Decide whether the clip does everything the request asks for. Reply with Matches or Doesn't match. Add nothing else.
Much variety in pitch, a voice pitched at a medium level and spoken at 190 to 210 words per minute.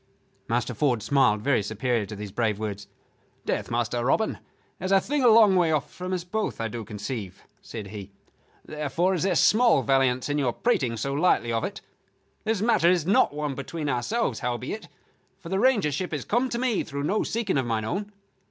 Matches